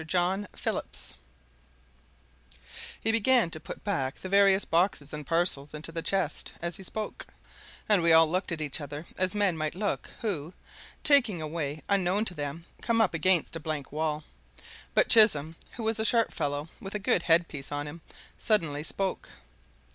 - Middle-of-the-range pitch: Yes, medium, 170 Hz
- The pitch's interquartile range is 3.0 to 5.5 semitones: Yes, average, 4.6 semitones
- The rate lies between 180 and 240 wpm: No, average, 170 wpm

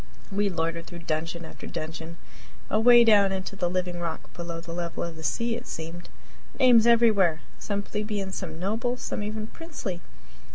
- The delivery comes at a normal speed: Yes, average, 165 wpm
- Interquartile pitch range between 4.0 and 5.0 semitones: Yes, average, 4.4 semitones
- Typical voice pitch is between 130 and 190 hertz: Yes, medium, 185 Hz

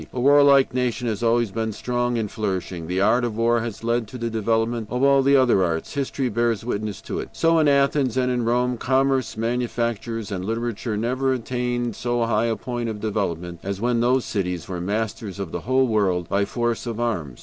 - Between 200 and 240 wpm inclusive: Yes, fast, 205 wpm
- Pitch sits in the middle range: No, low, 115 Hz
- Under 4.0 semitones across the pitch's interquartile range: Yes, average, 2.8 semitones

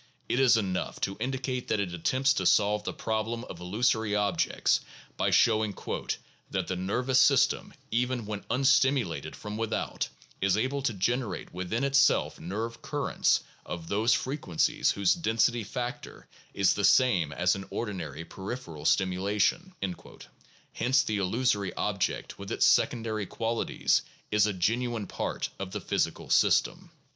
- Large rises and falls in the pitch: No, average, 4.2 semitones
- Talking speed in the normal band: Yes, average, 150 wpm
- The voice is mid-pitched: No, low, 110 Hz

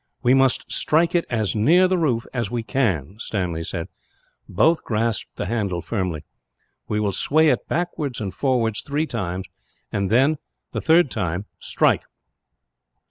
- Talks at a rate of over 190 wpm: No, average, 145 wpm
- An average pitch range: No, wide, 6.7 semitones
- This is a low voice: Yes, low, 115 Hz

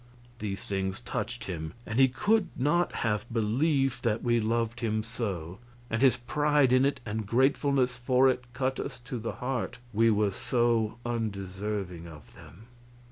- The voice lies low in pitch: Yes, low, 115 Hz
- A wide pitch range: No, average, 3.4 semitones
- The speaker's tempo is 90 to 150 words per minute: No, average, 160 wpm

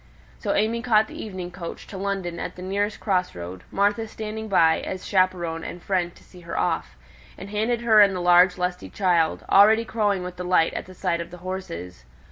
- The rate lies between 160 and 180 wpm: No, fast, 205 wpm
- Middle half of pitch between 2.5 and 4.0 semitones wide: Yes, average, 2.8 semitones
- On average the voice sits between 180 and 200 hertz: Yes, medium, 185 Hz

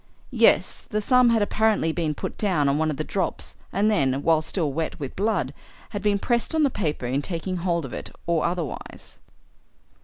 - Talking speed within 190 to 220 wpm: Yes, average, 195 wpm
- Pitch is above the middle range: No, medium, 170 Hz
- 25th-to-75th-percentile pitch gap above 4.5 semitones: Yes, wide, 5.4 semitones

